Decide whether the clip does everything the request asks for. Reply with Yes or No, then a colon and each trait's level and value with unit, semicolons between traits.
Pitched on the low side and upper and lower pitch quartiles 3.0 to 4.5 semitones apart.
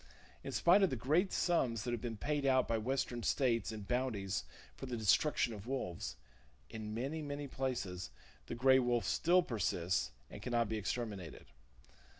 Yes: low, 120 Hz; average, 4.0 semitones